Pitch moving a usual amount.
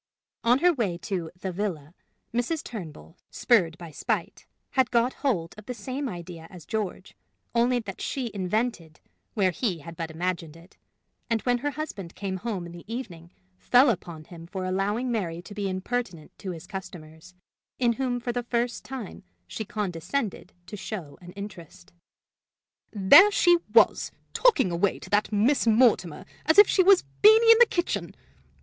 No: wide, 5.9 semitones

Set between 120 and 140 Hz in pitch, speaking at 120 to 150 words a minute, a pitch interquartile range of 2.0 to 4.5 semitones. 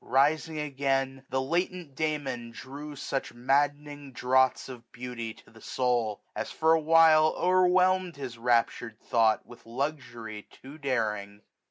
Yes: low, 135 Hz; average, 140 wpm; average, 4.2 semitones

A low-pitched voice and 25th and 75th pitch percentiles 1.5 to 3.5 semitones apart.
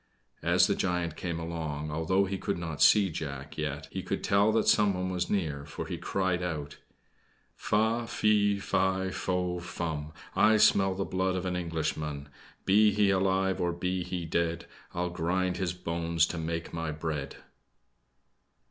Yes: very low, 90 Hz; average, 2.8 semitones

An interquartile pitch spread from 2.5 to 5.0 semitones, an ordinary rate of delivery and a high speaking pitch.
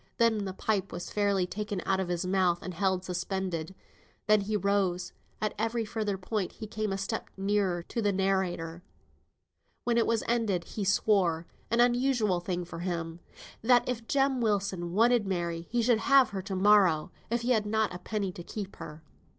Yes: average, 3.4 semitones; average, 190 wpm; high, 195 Hz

